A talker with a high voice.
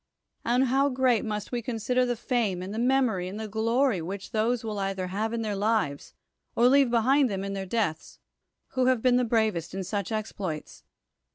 Yes: high, 220 Hz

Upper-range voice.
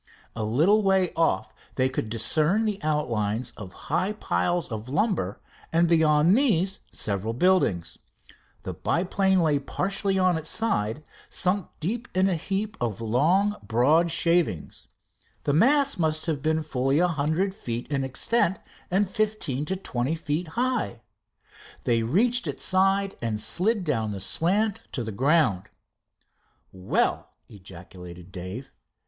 No: medium, 160 Hz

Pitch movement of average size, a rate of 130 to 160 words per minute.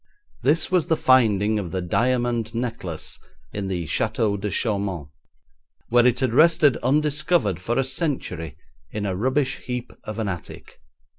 Yes: average, 4.9 semitones; average, 150 wpm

